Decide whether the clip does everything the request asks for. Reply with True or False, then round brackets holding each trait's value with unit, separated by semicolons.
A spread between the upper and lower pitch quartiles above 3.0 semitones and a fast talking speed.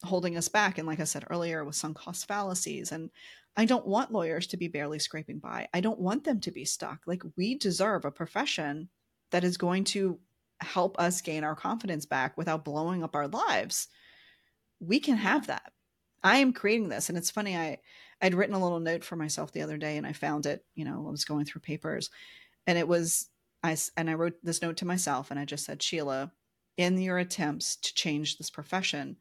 True (3.4 semitones; 215 wpm)